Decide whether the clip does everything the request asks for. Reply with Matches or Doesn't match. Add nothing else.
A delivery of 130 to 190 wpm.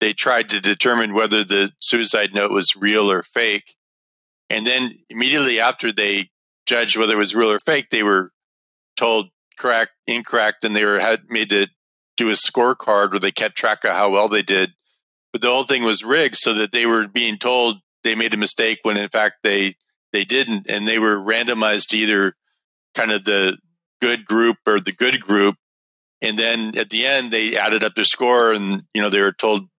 Doesn't match